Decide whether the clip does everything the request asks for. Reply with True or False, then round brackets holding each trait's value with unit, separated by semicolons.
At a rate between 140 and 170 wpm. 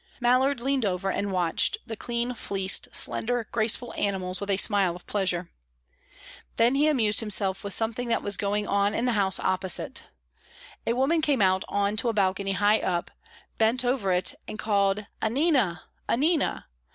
True (165 wpm)